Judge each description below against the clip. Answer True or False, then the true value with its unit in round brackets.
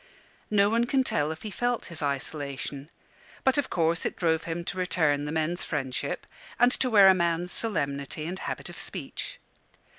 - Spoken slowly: False (180 wpm)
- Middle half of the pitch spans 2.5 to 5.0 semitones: False (5.5 semitones)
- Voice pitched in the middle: True (170 Hz)